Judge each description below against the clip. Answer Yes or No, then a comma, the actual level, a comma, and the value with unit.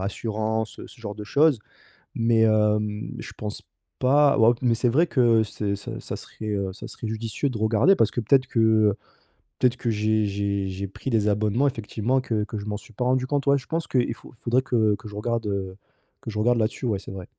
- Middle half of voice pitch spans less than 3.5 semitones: Yes, average, 2.9 semitones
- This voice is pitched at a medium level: No, low, 110 Hz